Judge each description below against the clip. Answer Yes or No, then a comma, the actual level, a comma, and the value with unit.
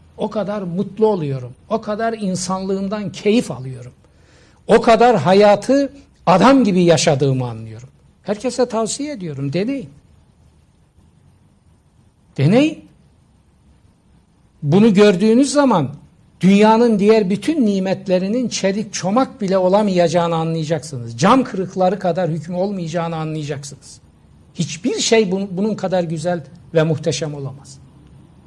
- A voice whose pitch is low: No, high, 190 Hz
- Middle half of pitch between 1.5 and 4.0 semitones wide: No, average, 5.1 semitones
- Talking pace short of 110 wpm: Yes, average, 100 wpm